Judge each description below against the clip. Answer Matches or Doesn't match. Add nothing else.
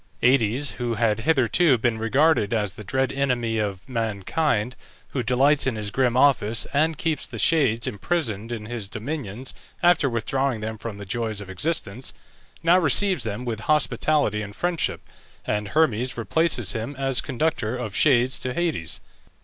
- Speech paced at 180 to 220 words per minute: Doesn't match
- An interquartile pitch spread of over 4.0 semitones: Matches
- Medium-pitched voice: Doesn't match